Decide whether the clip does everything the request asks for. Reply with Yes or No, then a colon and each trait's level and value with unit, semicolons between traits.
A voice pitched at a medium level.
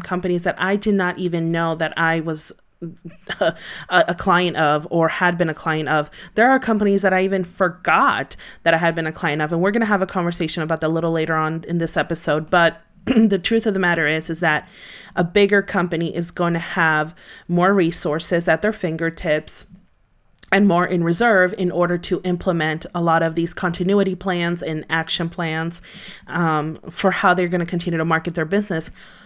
Yes: medium, 175 Hz